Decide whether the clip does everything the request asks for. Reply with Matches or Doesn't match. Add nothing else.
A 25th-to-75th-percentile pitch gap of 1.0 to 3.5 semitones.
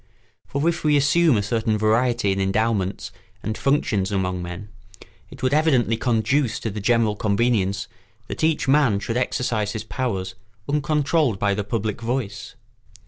Doesn't match